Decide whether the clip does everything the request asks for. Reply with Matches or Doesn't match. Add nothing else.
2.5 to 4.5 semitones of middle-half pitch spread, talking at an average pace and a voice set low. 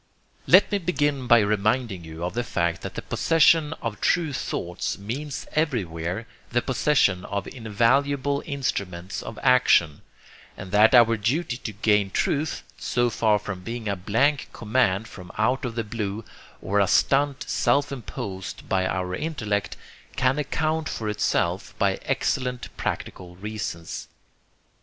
Doesn't match